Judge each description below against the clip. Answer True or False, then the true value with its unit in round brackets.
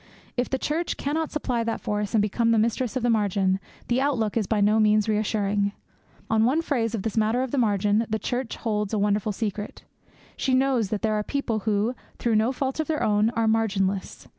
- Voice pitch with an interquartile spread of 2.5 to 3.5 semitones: True (2.9 semitones)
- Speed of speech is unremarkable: False (215 wpm)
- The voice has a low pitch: False (220 Hz)